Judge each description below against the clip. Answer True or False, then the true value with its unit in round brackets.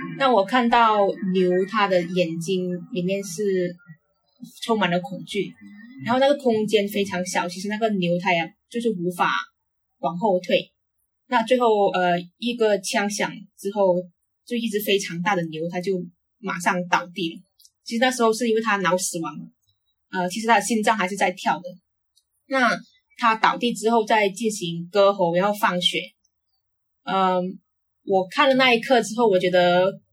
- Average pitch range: True (4.0 semitones)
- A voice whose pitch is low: False (195 Hz)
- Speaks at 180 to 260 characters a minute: True (235 characters per minute)